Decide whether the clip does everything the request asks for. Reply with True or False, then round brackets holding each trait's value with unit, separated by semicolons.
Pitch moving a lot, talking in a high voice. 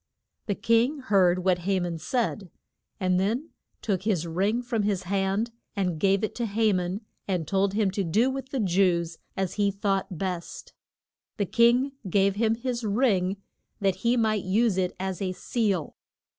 False (3.5 semitones; 195 Hz)